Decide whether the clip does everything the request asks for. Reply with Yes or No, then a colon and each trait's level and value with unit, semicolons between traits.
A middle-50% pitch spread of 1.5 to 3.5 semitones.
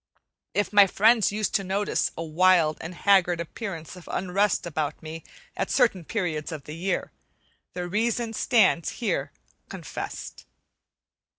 No: average, 3.9 semitones